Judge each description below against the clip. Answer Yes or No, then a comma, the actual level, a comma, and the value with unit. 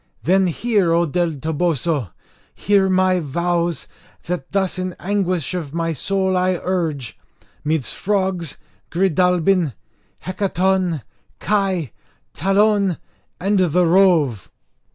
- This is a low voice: No, medium, 180 Hz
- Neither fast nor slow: No, slow, 105 wpm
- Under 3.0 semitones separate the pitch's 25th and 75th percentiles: Yes, narrow, 2.6 semitones